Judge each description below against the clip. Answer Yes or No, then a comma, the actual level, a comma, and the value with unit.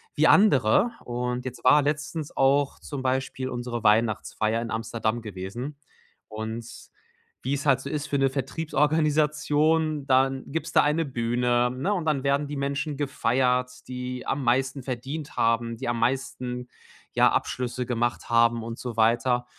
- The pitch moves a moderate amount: Yes, average, 3.2 semitones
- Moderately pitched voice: No, low, 130 Hz